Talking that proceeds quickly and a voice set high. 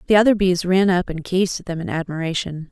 No: fast, 245 wpm; medium, 180 Hz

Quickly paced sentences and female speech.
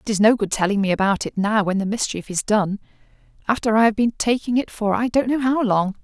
Yes: fast, 250 wpm; female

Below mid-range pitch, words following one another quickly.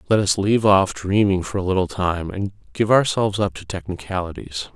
No: very low, 95 Hz; average, 190 wpm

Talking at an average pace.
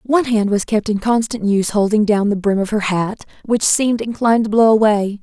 No: fast, 230 wpm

